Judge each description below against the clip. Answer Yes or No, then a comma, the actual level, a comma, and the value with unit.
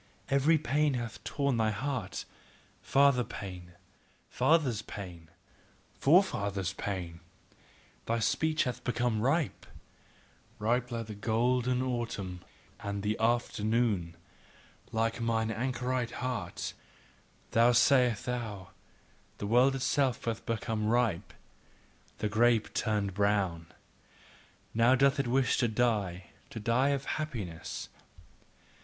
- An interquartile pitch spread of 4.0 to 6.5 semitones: No, average, 3.5 semitones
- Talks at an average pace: No, slow, 110 wpm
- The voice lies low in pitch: Yes, low, 115 Hz